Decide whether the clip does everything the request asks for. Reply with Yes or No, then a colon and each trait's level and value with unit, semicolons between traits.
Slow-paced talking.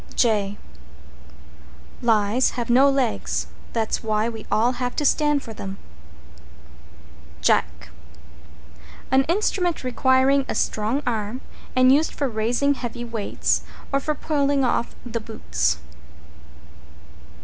Yes: slow, 115 wpm